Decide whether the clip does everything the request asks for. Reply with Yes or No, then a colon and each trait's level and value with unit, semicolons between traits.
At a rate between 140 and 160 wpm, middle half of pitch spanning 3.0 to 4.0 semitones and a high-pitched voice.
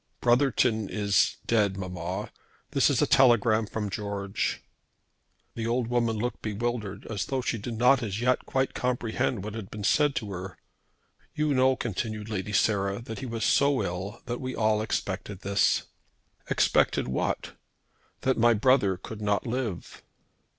No: average, 155 wpm; average, 3.3 semitones; low, 110 Hz